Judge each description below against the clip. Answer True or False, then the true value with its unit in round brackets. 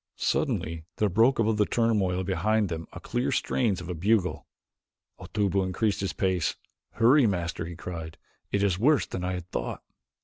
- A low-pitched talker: True (95 Hz)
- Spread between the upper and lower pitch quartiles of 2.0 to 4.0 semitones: True (3.7 semitones)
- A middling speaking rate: True (170 wpm)